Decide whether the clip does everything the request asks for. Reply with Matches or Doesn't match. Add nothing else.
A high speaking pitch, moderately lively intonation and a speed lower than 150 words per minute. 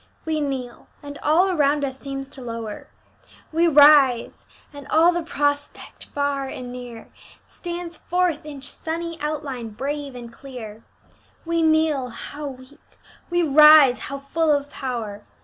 Matches